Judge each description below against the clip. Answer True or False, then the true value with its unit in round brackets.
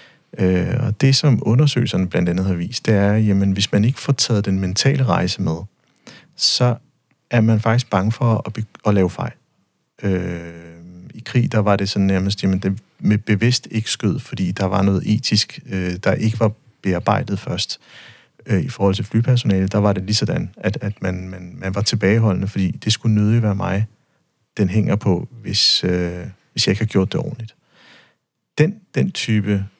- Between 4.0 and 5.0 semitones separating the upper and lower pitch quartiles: False (3.3 semitones)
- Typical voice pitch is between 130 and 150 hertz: False (105 Hz)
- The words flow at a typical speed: True (190 wpm)